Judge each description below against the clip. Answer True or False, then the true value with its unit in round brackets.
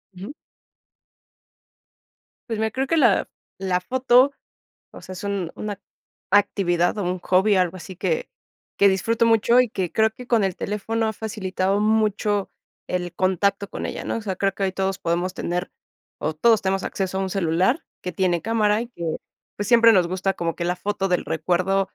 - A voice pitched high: True (195 Hz)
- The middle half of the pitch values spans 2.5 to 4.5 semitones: True (3.1 semitones)